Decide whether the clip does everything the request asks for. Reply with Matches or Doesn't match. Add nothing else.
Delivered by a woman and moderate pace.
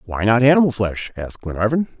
Doesn't match